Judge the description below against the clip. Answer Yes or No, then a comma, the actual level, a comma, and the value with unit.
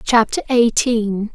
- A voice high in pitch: Yes, high, 230 Hz